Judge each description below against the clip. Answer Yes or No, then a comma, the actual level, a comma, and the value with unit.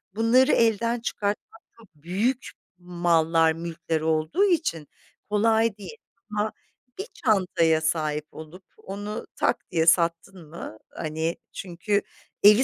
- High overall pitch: No, medium, 180 Hz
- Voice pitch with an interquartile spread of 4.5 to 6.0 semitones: Yes, average, 5.3 semitones